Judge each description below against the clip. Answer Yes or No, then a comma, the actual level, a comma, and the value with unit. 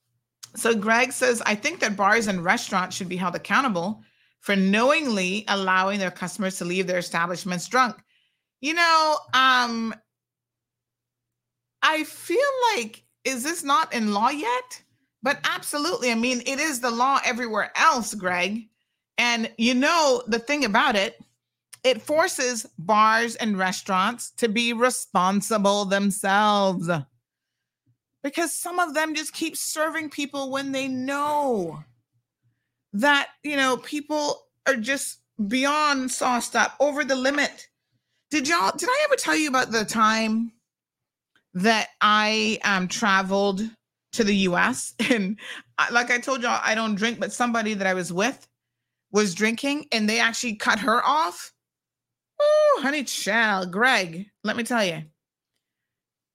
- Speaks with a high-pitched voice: Yes, high, 230 Hz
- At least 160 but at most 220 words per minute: No, average, 140 wpm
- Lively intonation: Yes, wide, 6.0 semitones